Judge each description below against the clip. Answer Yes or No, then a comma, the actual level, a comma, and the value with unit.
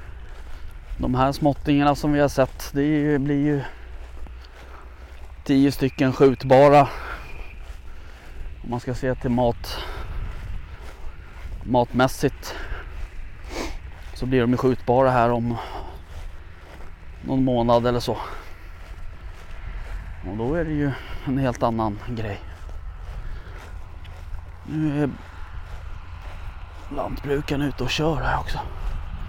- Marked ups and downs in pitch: Yes, wide, 8.1 semitones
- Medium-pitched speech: No, very low, 90 Hz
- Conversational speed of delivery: No, slow, 95 wpm